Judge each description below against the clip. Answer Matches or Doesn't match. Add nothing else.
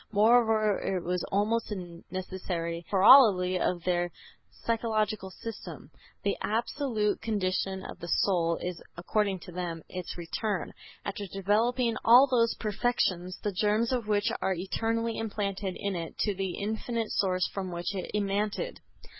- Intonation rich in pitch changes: Doesn't match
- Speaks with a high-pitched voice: Matches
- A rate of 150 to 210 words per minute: Doesn't match